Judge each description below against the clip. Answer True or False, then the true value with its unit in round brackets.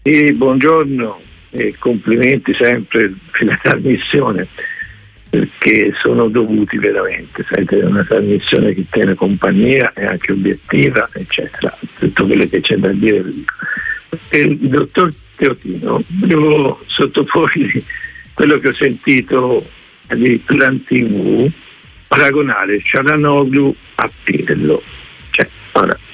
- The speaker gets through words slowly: True (110 wpm)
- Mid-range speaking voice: True (150 Hz)